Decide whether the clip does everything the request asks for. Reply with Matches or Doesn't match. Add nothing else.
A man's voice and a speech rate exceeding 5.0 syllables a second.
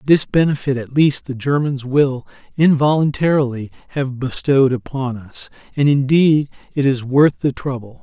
Doesn't match